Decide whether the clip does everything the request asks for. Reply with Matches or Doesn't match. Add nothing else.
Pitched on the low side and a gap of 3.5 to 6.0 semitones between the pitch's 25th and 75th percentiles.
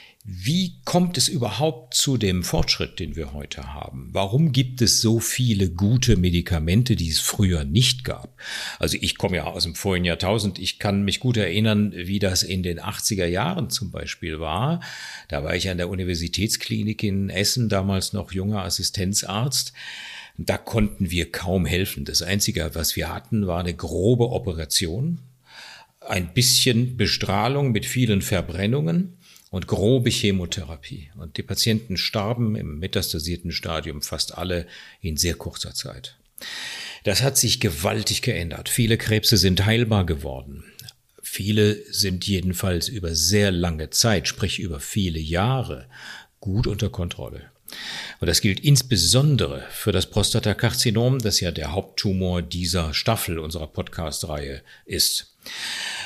Matches